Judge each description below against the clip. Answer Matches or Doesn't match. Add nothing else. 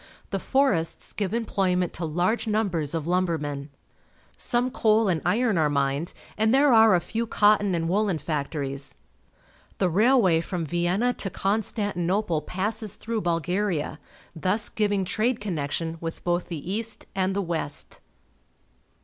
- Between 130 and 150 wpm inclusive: Matches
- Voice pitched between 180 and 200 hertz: Matches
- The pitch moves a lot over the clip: Doesn't match